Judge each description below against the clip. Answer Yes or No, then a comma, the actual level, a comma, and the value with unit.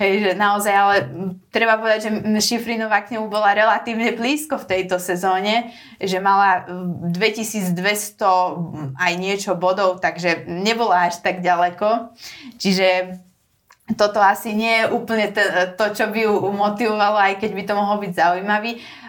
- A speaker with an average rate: Yes, average, 140 wpm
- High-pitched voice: Yes, high, 205 Hz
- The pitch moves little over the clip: No, average, 3.1 semitones